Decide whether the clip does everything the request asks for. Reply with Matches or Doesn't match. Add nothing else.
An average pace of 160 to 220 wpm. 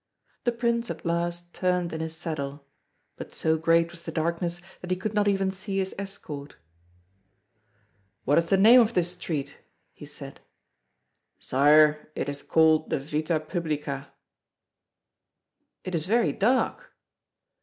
Doesn't match